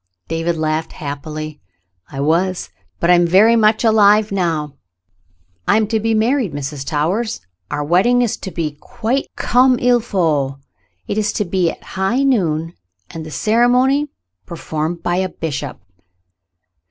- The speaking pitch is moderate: Yes, medium, 180 Hz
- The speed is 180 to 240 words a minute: No, average, 155 wpm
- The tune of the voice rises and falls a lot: Yes, wide, 6.1 semitones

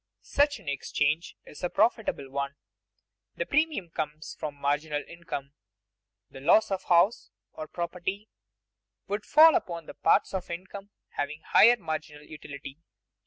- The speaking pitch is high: No, medium, 170 Hz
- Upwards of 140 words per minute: No, slow, 135 wpm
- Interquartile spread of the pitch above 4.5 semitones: Yes, average, 5.3 semitones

